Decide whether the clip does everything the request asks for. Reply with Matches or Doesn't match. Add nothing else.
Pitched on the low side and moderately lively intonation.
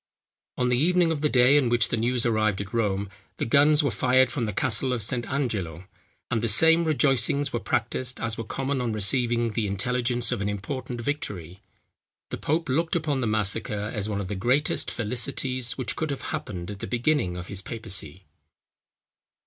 Matches